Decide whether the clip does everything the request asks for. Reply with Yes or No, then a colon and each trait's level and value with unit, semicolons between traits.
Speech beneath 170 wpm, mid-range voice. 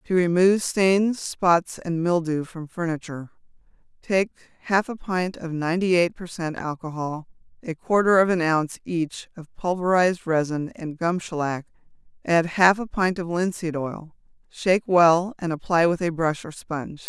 Yes: average, 160 wpm; medium, 170 Hz